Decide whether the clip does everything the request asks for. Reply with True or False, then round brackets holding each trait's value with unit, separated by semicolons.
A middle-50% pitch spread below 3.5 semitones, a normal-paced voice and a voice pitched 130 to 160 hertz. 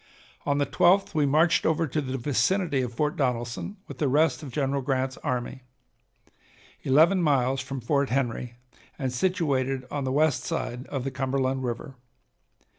True (2.6 semitones; 160 wpm; 135 Hz)